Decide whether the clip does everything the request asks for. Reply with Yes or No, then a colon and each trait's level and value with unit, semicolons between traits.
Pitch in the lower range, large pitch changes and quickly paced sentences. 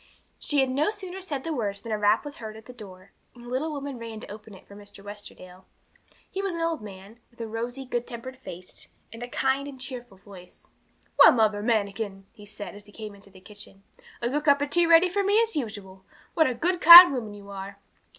No: high, 230 Hz; wide, 5.8 semitones; fast, 235 wpm